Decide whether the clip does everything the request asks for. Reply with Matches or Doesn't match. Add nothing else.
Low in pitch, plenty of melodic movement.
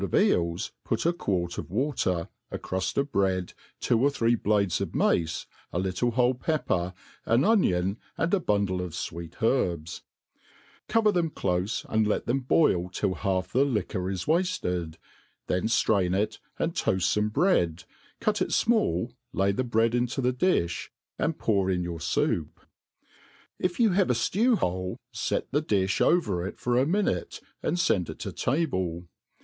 Matches